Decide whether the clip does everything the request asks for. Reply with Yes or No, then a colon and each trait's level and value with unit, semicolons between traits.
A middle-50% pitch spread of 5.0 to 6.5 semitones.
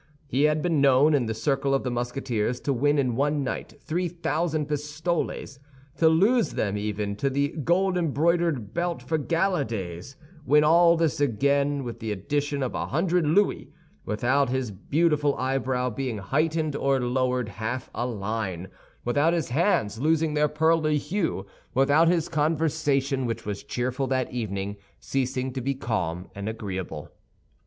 No: average, 4.5 semitones